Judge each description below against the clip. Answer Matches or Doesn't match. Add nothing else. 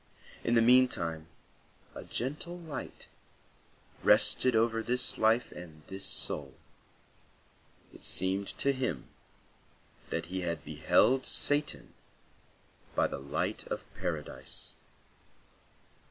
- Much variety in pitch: Matches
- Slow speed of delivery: Matches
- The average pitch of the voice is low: Matches